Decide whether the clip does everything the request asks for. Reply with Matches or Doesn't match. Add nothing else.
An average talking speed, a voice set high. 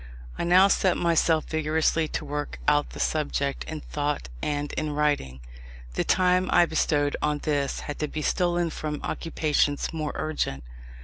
Doesn't match